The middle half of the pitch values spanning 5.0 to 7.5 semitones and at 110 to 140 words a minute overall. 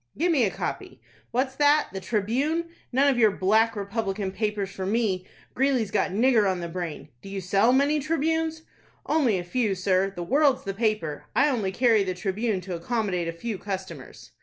No: wide, 5.4 semitones; average, 185 wpm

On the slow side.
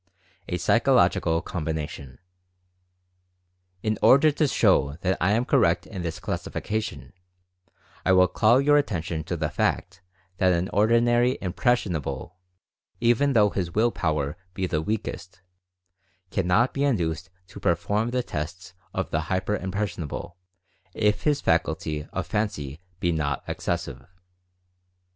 Yes: slow, 130 wpm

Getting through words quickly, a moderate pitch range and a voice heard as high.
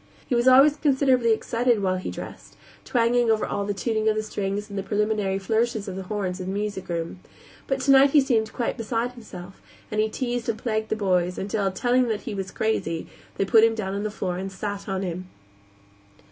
Yes: fast, 220 wpm; average, 3.5 semitones; high, 215 Hz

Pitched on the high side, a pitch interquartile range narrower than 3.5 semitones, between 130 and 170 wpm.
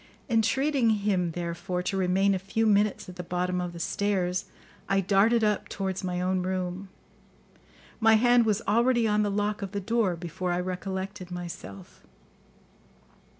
Yes: high, 195 Hz; average, 2.8 semitones; average, 155 wpm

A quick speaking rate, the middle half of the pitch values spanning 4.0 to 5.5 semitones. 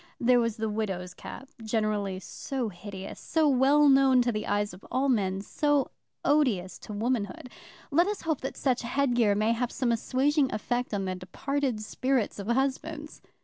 No: average, 170 wpm; average, 4.7 semitones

